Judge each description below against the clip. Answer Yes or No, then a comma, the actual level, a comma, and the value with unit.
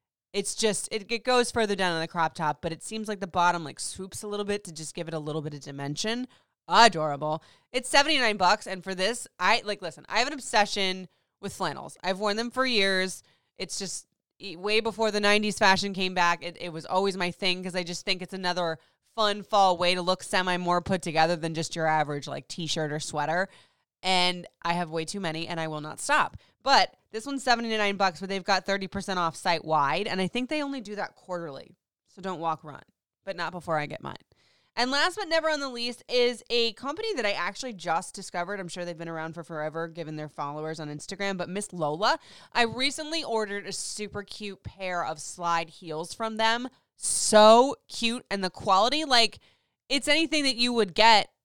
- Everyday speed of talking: No, fast, 215 wpm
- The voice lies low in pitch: No, high, 190 Hz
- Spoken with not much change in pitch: No, average, 4.7 semitones